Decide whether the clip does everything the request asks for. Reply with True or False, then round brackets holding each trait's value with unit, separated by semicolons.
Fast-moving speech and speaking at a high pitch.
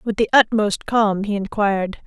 False (175 wpm; 215 Hz)